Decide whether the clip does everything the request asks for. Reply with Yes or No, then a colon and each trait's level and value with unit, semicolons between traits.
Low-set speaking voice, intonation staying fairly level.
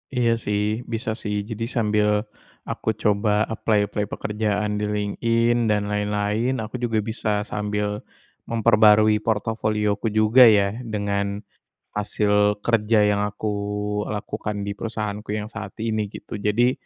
Yes: low, 105 Hz; narrow, 1.3 semitones